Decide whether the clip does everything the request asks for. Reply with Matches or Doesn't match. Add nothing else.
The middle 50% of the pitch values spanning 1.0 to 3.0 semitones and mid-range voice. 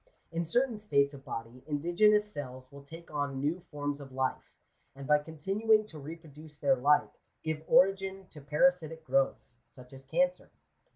Doesn't match